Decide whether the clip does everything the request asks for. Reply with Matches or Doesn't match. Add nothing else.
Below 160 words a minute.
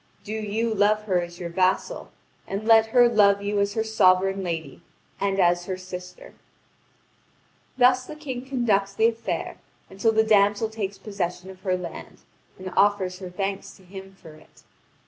Doesn't match